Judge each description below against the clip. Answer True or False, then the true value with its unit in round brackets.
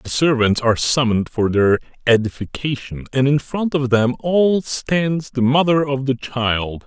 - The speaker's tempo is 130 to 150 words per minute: False (165 wpm)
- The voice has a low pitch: True (130 Hz)